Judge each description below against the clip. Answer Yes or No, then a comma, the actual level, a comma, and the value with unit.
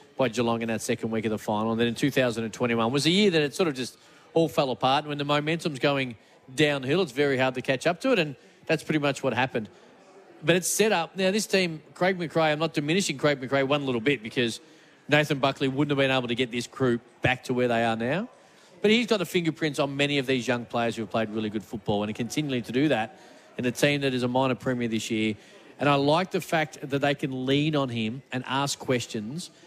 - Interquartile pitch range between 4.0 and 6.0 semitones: Yes, average, 4.3 semitones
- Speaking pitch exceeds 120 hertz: Yes, medium, 140 Hz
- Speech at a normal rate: No, fast, 255 wpm